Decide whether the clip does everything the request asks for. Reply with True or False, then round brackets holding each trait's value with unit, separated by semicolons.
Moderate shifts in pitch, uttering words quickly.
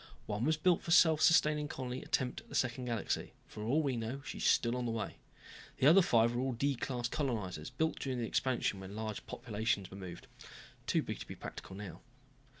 True (4.5 semitones; 215 wpm)